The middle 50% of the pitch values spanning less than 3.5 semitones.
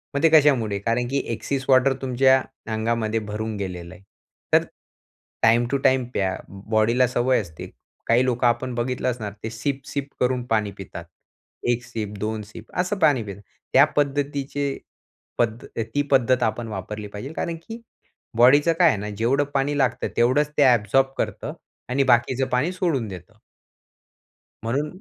No: average, 3.8 semitones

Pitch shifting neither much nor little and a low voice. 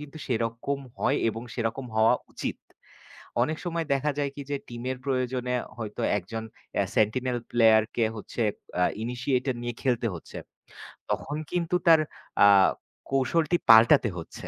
Yes: average, 3.7 semitones; low, 125 Hz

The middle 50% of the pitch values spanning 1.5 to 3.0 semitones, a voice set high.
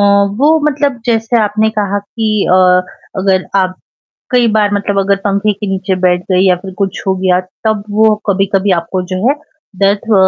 Yes: narrow, 2.4 semitones; high, 200 Hz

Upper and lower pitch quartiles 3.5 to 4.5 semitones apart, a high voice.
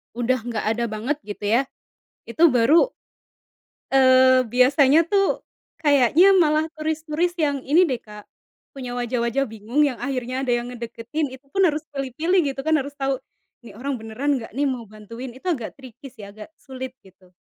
Yes: average, 3.8 semitones; very high, 260 Hz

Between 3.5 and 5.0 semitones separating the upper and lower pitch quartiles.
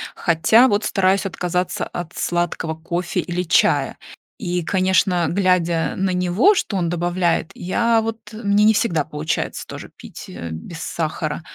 No: average, 2.8 semitones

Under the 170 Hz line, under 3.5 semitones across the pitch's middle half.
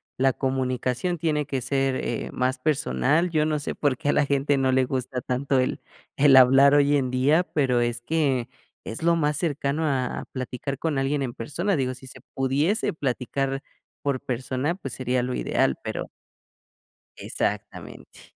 Yes: low, 135 Hz; narrow, 2.5 semitones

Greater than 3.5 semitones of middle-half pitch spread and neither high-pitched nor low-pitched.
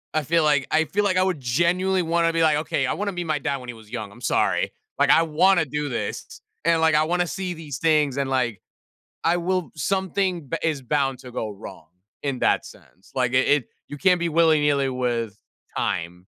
Yes: average, 5.0 semitones; medium, 150 Hz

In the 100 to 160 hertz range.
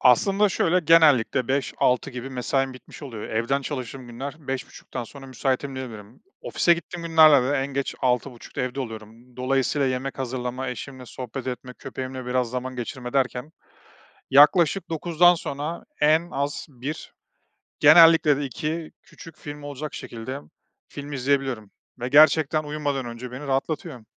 Yes: low, 135 Hz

